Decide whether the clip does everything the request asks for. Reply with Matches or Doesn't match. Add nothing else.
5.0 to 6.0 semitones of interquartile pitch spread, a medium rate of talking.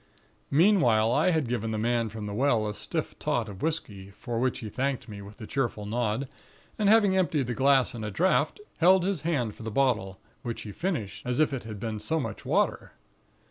Doesn't match